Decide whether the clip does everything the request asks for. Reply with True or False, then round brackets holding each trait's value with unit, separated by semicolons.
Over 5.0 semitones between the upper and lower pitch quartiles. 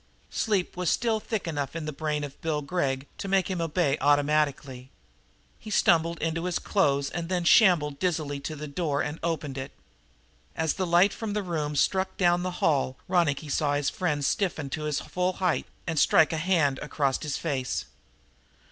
False (3.8 semitones)